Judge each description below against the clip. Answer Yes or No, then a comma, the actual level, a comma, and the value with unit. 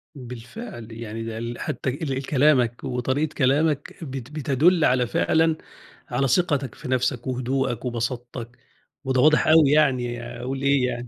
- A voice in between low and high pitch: No, low, 130 Hz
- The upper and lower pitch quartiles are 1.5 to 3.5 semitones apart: Yes, average, 3.2 semitones